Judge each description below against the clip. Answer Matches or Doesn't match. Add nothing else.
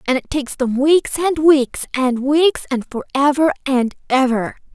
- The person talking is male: Doesn't match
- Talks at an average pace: Matches